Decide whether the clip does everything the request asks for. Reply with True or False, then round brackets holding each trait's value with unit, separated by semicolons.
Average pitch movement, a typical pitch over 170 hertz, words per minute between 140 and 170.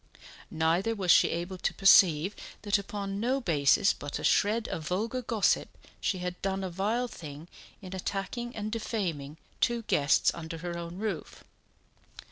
True (4.2 semitones; 190 Hz; 155 wpm)